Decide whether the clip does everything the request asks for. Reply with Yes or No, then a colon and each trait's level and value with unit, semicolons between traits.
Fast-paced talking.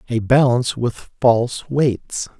No: slow, 125 wpm